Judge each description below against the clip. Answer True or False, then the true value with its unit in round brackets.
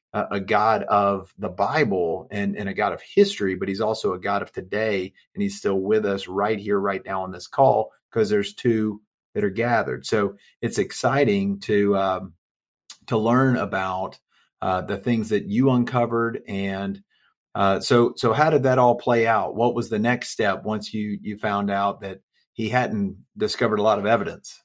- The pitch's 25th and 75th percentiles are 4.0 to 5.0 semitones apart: False (3.6 semitones)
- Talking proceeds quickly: False (190 wpm)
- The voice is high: False (105 Hz)